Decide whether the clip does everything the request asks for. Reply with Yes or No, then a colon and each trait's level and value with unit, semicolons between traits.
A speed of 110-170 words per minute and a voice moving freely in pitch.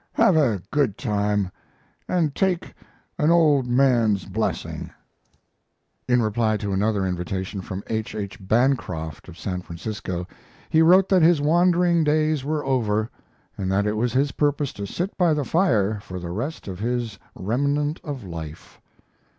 Yes: average, 150 wpm; wide, 6.9 semitones